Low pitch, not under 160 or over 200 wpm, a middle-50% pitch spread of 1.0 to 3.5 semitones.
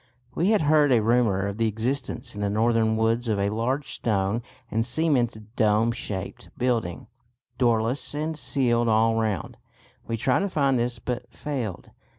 Yes: low, 115 Hz; average, 165 wpm; average, 2.8 semitones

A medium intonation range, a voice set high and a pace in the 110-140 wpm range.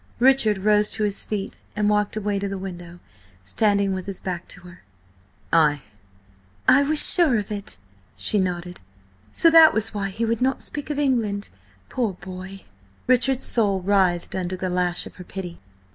No: average, 3.6 semitones; high, 200 Hz; average, 175 wpm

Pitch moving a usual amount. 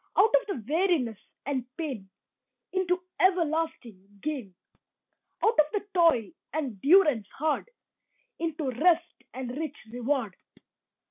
No: wide, 5.9 semitones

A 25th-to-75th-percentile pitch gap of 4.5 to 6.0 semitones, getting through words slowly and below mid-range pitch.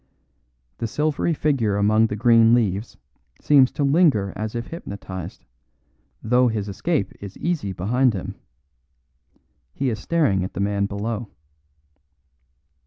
Yes: average, 4.8 semitones; slow, 125 wpm; low, 110 Hz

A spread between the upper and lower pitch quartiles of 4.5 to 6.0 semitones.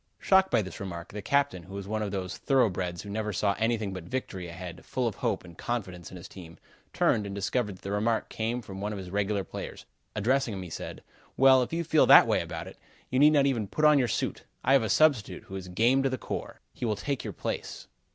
Yes: average, 5.3 semitones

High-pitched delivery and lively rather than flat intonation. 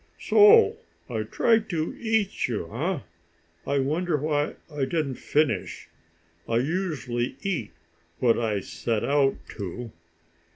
No: medium, 145 Hz; wide, 6.9 semitones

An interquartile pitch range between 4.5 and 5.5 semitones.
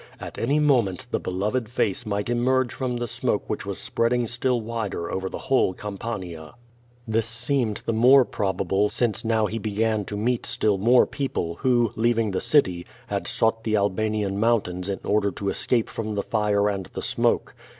No: average, 3.0 semitones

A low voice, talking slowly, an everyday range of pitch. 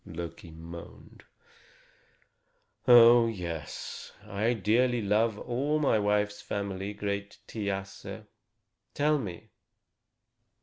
Yes: low, 105 Hz; slow, 75 wpm; average, 3.2 semitones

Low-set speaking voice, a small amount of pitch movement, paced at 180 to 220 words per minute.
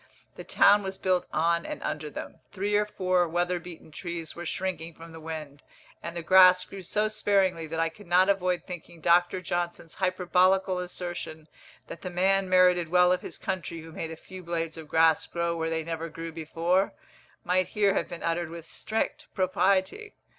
No: medium, 175 Hz; narrow, 2.1 semitones; average, 190 wpm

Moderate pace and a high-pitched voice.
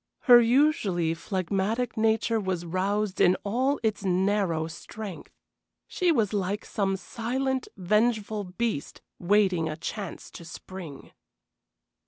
No: slow, 115 wpm; high, 205 Hz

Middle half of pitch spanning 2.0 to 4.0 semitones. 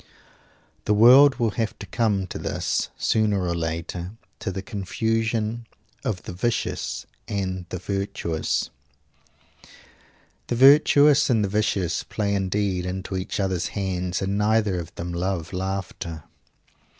Yes: average, 3.3 semitones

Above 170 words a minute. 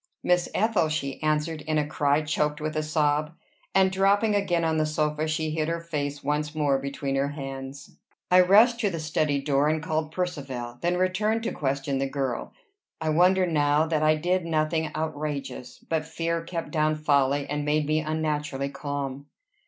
Yes: average, 180 wpm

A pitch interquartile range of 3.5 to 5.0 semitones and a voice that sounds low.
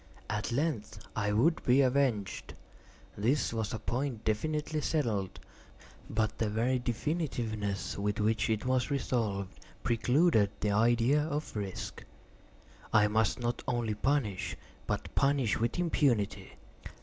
Yes: average, 4.7 semitones; low, 115 Hz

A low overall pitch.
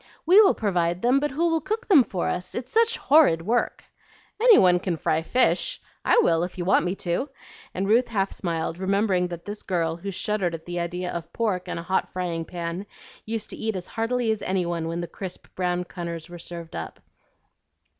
No: medium, 185 Hz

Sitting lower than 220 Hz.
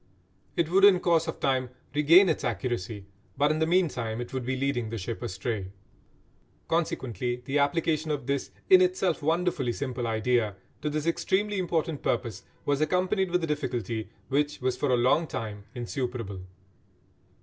Yes: medium, 140 Hz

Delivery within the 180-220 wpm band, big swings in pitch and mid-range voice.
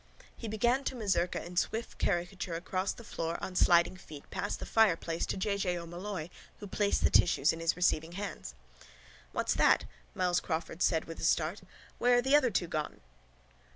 No: average, 185 wpm; average, 3.7 semitones; medium, 180 Hz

